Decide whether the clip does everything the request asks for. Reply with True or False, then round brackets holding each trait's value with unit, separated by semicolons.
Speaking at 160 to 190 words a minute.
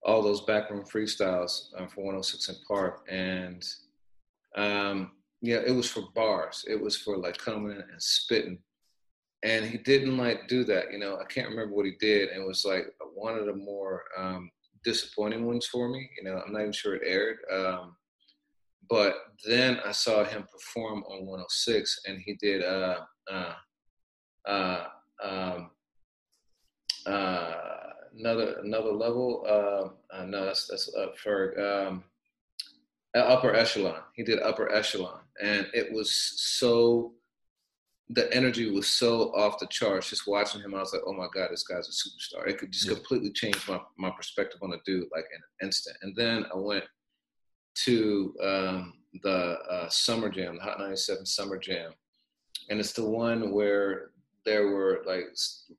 True (170 wpm)